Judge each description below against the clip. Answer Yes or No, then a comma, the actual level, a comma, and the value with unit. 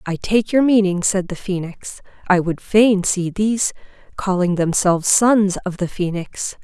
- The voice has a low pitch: No, high, 190 Hz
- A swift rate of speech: No, average, 165 wpm